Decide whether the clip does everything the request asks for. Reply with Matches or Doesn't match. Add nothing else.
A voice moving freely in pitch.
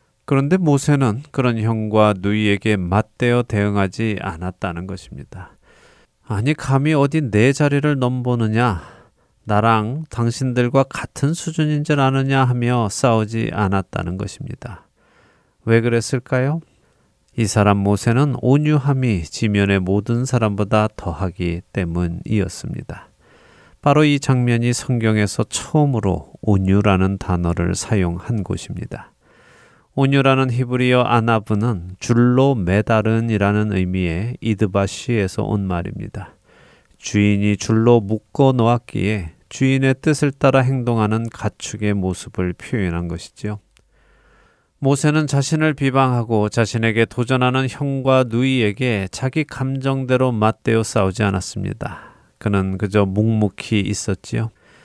Doesn't match